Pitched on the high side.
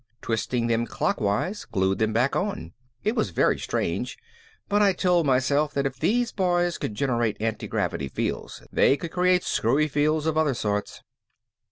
No: medium, 140 Hz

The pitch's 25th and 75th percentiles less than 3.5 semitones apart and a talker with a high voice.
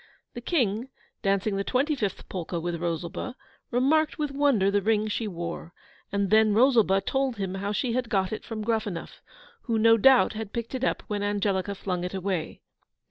No: average, 3.9 semitones; high, 210 Hz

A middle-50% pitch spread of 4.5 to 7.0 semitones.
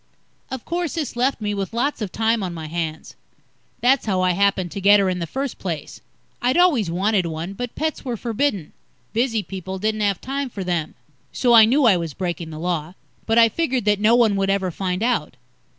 Yes: average, 5.0 semitones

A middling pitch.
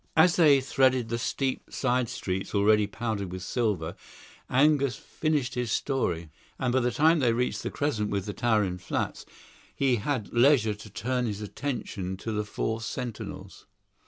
No: low, 115 Hz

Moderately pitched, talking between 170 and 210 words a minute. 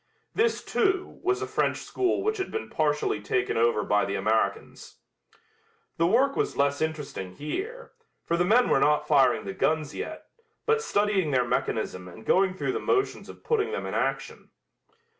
Yes: medium, 160 Hz; average, 175 wpm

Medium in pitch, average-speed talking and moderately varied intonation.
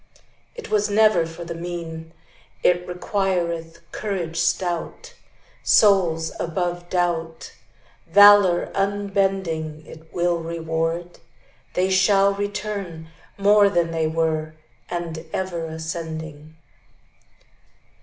No: medium, 175 Hz; slow, 95 wpm; average, 3.1 semitones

